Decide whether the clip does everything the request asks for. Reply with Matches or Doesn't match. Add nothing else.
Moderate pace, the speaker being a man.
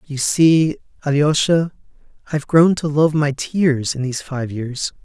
Matches